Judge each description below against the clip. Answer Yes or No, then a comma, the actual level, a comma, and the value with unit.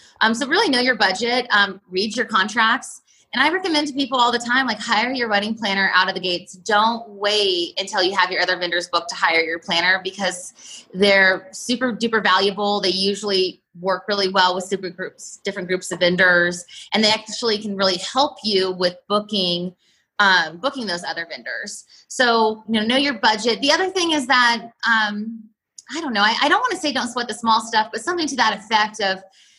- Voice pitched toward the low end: No, high, 210 Hz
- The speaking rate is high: Yes, fast, 210 wpm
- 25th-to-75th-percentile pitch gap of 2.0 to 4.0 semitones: No, average, 4.4 semitones